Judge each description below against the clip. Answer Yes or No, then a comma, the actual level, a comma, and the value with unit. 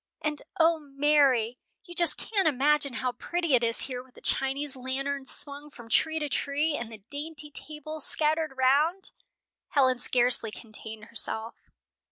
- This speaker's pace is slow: No, average, 155 wpm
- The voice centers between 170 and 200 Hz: No, very high, 280 Hz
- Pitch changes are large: No, average, 3.4 semitones